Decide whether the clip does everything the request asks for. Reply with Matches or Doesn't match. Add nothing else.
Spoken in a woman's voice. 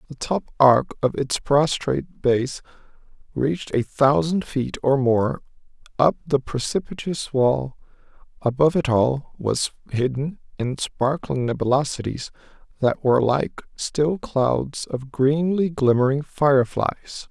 Doesn't match